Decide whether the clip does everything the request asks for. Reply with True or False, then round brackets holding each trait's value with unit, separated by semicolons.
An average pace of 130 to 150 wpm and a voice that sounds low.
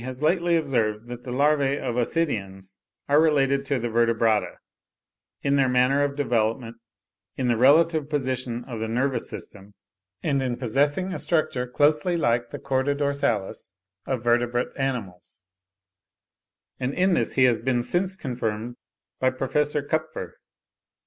True (140 wpm; 130 Hz)